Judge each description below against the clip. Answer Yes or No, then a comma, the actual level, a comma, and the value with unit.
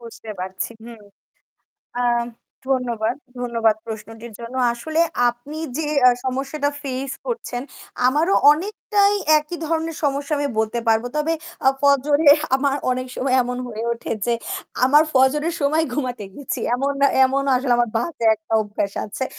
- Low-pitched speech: No, very high, 260 Hz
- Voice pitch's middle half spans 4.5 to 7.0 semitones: No, average, 4.0 semitones